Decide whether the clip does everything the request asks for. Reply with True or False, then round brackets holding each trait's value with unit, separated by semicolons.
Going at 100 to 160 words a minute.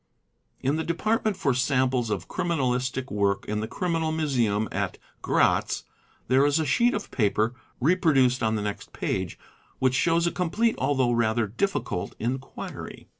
True (150 wpm)